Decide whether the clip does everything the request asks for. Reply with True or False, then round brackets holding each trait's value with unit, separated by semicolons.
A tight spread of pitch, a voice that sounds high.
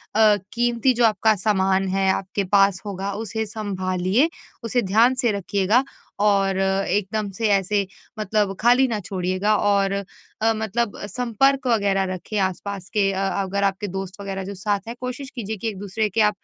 True (2.3 semitones; 200 Hz)